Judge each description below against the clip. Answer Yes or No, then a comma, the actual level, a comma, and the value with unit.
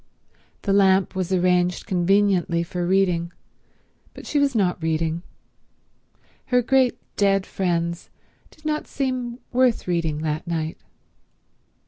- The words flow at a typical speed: No, slow, 115 wpm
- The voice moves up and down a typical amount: Yes, average, 4.9 semitones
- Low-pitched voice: No, medium, 185 Hz